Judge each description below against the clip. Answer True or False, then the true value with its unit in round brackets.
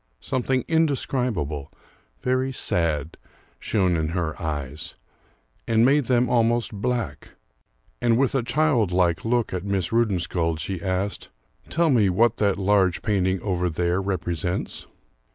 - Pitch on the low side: True (100 Hz)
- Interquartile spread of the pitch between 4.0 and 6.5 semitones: True (5.6 semitones)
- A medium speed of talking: False (125 wpm)